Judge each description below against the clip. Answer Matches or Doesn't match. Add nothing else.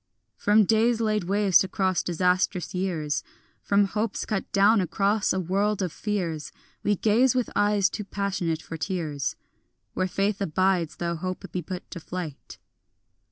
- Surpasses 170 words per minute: Doesn't match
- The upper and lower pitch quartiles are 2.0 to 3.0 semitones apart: Matches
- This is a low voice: Doesn't match